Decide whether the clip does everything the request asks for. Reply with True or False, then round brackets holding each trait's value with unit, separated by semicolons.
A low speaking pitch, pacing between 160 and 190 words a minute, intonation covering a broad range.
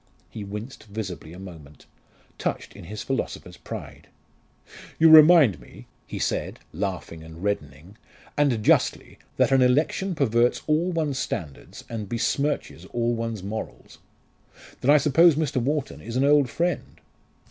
False (120 Hz; 140 wpm; 7.1 semitones)